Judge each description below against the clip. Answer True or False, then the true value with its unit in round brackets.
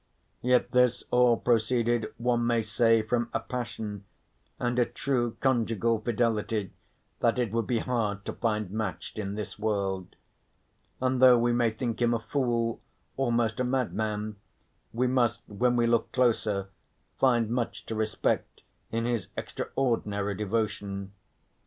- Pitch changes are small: True (2.2 semitones)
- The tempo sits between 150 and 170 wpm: False (140 wpm)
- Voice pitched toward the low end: True (115 Hz)